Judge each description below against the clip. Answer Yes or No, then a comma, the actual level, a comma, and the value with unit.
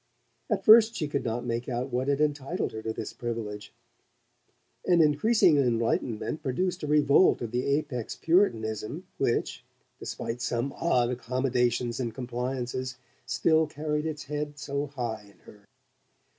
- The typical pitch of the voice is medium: No, low, 130 Hz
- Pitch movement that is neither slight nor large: Yes, average, 4.0 semitones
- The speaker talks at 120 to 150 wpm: Yes, average, 145 wpm